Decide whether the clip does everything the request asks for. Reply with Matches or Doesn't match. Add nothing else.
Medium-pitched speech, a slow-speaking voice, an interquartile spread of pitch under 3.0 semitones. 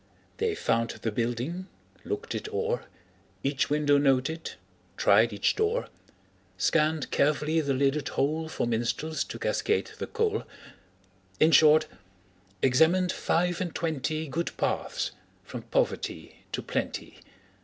Doesn't match